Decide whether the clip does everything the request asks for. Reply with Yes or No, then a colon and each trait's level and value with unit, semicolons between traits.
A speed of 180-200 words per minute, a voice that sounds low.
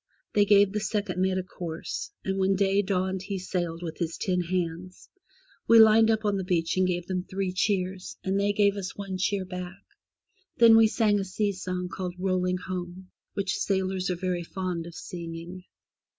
No: average, 190 wpm; medium, 185 Hz